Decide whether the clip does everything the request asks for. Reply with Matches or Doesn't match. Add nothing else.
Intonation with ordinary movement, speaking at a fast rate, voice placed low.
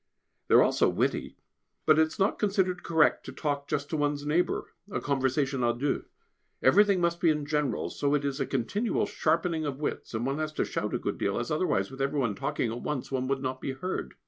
Doesn't match